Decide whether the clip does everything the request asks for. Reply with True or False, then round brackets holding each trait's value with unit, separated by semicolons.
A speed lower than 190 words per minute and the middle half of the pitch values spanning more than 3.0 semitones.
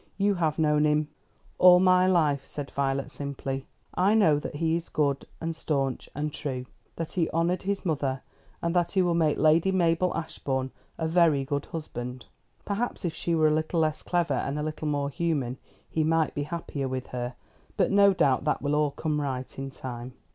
False (200 wpm; 3.4 semitones)